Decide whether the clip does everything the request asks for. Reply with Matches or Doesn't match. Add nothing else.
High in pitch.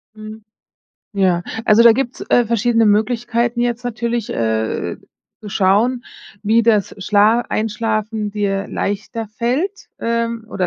Matches